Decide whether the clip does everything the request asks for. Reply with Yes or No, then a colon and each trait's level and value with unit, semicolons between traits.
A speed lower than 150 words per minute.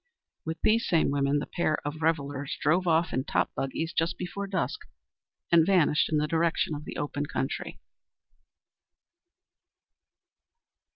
Yes: slow, 135 wpm